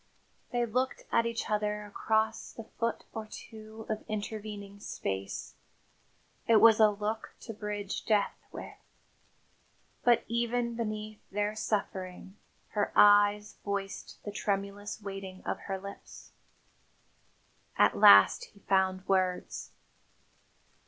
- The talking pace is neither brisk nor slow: No, slow, 115 wpm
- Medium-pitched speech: No, high, 210 Hz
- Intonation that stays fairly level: Yes, narrow, 1.7 semitones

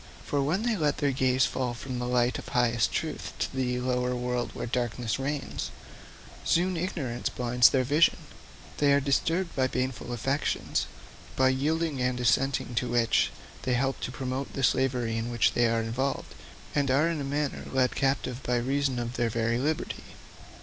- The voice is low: Yes, low, 130 Hz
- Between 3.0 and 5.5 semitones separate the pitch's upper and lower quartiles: No, narrow, 2.4 semitones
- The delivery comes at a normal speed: Yes, average, 175 wpm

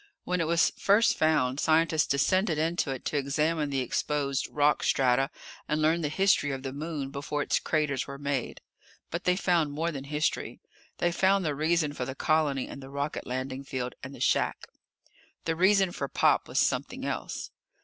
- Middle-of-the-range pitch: Yes, medium, 150 Hz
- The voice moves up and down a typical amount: Yes, average, 3.2 semitones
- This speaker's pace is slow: No, average, 185 wpm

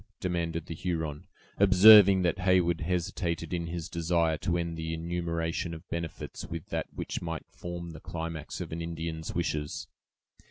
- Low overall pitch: Yes, very low, 85 Hz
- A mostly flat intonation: Yes, narrow, 1.2 semitones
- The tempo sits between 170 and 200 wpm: No, average, 155 wpm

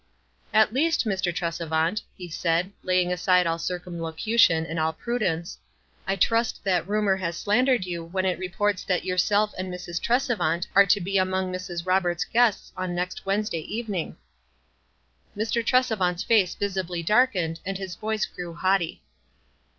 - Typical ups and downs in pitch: Yes, average, 3.2 semitones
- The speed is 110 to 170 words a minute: Yes, average, 155 wpm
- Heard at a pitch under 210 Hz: Yes, medium, 185 Hz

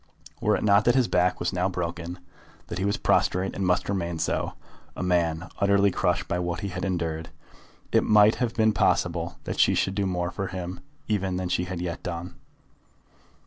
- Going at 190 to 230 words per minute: Yes, average, 195 wpm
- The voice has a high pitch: No, very low, 90 Hz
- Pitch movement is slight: Yes, narrow, 2.1 semitones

